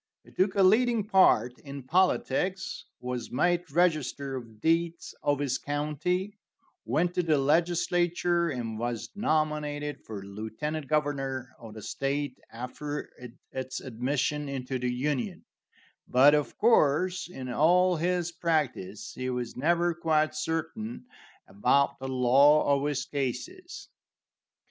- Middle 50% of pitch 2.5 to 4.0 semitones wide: No, average, 5.1 semitones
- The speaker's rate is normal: No, slow, 125 wpm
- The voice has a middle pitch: Yes, medium, 145 Hz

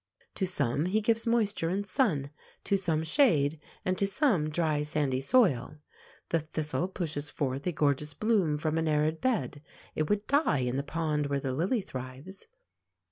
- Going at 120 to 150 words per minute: No, average, 170 wpm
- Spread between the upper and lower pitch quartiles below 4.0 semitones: No, average, 5.3 semitones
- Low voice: No, medium, 155 Hz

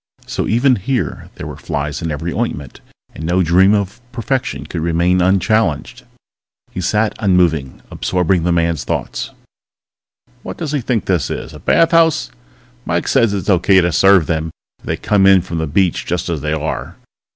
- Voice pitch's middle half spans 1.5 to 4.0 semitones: No, average, 4.5 semitones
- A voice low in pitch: Yes, very low, 90 Hz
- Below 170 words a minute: No, average, 175 wpm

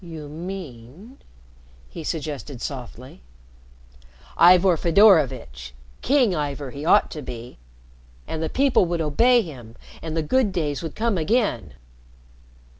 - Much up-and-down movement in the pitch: Yes, wide, 6.5 semitones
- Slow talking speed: Yes, slow, 125 wpm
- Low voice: No, medium, 155 Hz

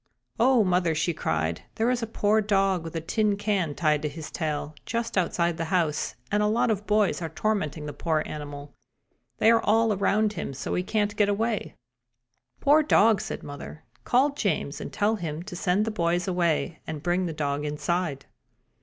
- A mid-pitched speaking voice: Yes, medium, 180 Hz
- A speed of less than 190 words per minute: No, average, 195 wpm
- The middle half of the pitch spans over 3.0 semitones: Yes, average, 5.3 semitones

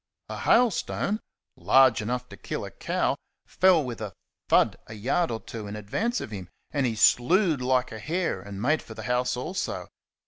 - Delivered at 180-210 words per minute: Yes, average, 185 wpm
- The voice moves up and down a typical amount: No, wide, 6.9 semitones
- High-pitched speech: No, low, 125 Hz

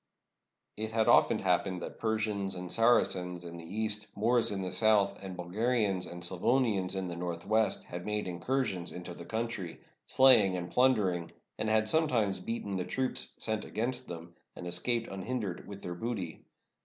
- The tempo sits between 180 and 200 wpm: No, average, 170 wpm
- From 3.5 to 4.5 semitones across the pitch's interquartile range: Yes, average, 4.0 semitones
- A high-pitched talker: No, low, 100 Hz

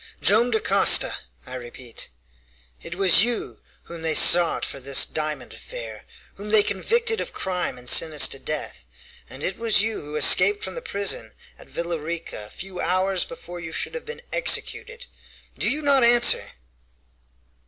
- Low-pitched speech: No, medium, 185 Hz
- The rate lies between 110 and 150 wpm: No, average, 165 wpm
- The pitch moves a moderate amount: No, wide, 6.7 semitones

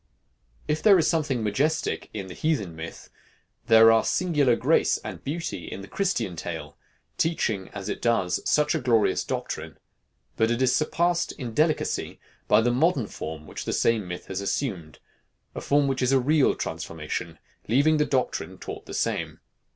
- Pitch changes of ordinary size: No, wide, 7.3 semitones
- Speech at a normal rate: Yes, average, 170 wpm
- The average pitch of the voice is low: Yes, low, 125 Hz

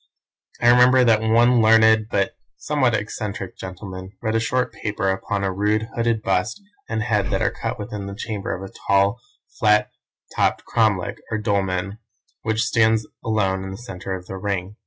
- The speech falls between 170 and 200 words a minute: Yes, average, 175 wpm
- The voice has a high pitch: No, low, 105 Hz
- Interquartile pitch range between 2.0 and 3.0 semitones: Yes, narrow, 2.6 semitones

